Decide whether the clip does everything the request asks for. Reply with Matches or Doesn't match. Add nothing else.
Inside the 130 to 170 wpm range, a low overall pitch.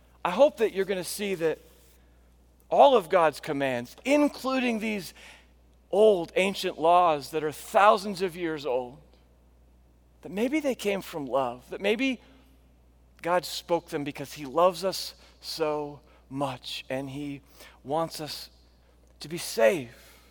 Doesn't match